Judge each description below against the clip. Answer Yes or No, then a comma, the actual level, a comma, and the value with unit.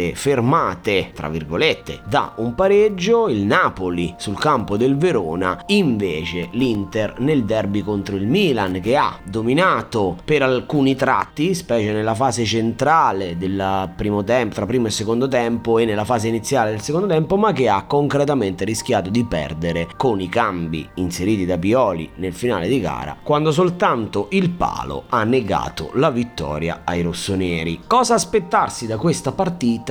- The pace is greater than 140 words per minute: Yes, average, 150 wpm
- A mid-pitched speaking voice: No, low, 115 Hz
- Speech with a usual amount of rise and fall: No, wide, 6.6 semitones